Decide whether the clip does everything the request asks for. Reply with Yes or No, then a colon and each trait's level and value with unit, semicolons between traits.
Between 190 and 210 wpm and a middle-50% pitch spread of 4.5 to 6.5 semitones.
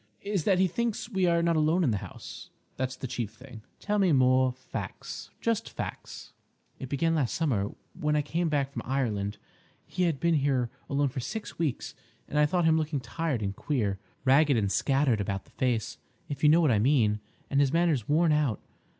Yes: average, 195 wpm; average, 5.0 semitones